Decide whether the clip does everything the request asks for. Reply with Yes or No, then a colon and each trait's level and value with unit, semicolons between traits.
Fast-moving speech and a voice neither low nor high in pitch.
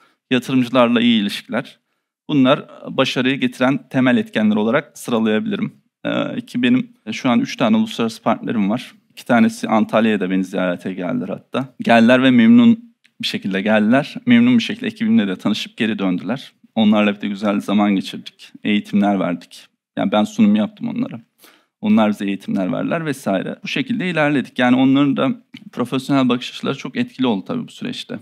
Yes: fast, 155 wpm; medium, 145 Hz